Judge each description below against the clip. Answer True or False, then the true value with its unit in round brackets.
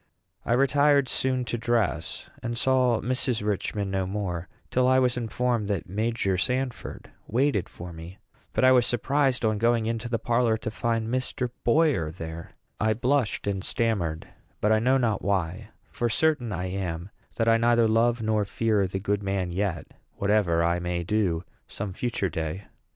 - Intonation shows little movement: False (4.1 semitones)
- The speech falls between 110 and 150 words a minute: False (170 wpm)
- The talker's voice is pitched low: True (110 Hz)